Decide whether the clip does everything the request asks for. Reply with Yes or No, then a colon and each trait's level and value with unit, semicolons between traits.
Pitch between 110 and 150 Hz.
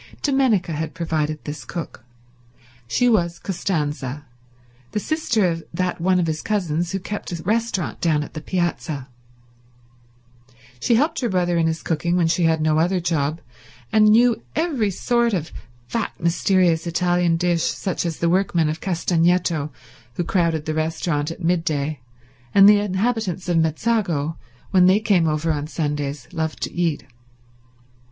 No: medium, 170 Hz